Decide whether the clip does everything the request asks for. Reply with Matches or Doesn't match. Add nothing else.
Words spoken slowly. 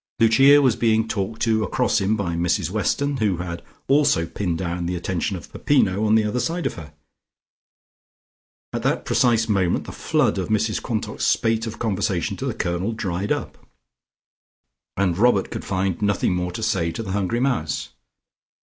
Doesn't match